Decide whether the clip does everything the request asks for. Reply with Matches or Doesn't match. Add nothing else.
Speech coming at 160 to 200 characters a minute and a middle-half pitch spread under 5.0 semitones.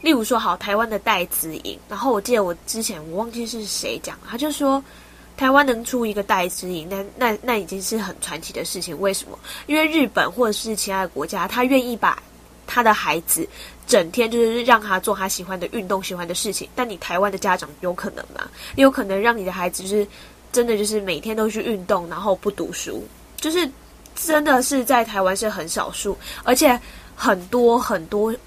Doesn't match